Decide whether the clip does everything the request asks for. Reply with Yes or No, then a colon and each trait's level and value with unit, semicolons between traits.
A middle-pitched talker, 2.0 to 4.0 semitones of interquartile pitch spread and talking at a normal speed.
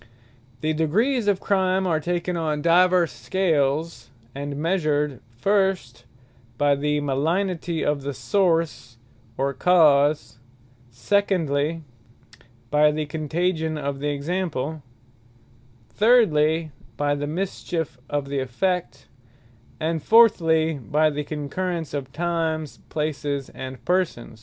No: medium, 155 Hz; average, 3.7 semitones; slow, 110 wpm